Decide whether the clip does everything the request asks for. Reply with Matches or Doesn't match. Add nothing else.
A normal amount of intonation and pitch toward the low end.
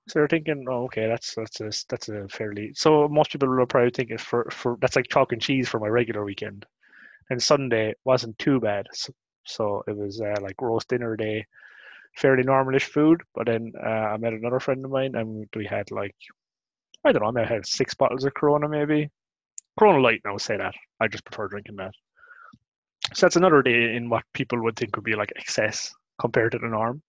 Matches